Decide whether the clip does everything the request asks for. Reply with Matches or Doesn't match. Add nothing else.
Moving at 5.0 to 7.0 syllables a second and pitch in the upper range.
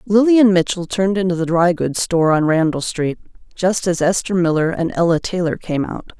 Doesn't match